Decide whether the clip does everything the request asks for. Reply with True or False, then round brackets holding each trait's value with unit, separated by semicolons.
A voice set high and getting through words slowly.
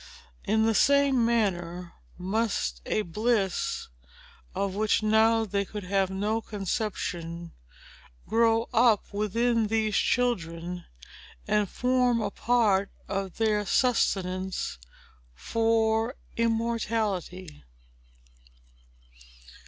True (215 Hz; 90 wpm)